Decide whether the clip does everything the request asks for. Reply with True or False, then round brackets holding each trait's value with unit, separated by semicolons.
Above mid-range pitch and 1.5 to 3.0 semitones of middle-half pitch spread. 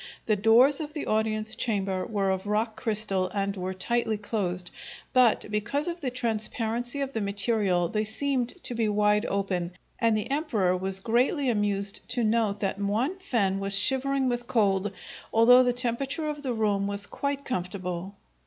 False (220 Hz; 3.8 semitones)